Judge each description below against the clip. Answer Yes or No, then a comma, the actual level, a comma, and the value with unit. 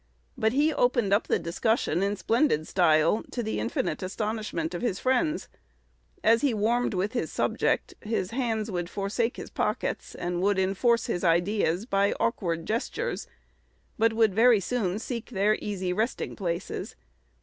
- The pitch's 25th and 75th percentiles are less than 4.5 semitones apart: Yes, average, 4.1 semitones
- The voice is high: Yes, high, 210 Hz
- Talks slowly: No, average, 155 wpm